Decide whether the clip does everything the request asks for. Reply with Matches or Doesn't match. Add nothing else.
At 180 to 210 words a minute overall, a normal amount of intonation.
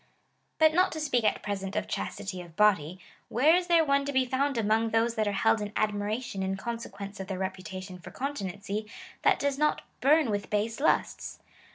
Doesn't match